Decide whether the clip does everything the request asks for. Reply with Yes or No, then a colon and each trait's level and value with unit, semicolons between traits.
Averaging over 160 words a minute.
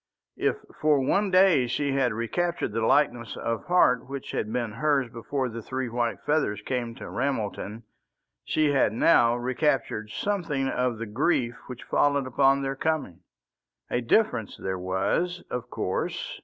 No: average, 155 wpm